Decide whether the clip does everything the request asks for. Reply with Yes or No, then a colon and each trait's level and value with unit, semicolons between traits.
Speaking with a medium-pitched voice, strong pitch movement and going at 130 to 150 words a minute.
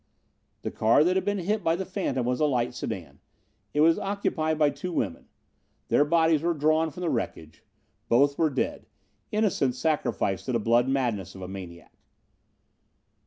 No: medium, 145 Hz; wide, 6.0 semitones; average, 170 wpm